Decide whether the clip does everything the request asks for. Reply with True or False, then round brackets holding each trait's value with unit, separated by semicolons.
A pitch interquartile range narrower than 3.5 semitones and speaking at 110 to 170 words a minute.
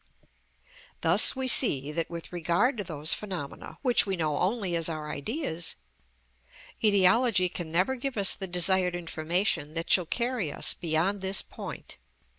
False (4.0 semitones; 150 wpm)